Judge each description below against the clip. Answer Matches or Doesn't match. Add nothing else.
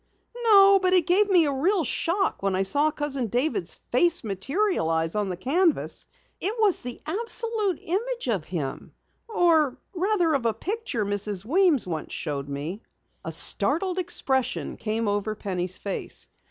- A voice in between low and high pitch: Doesn't match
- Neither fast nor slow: Matches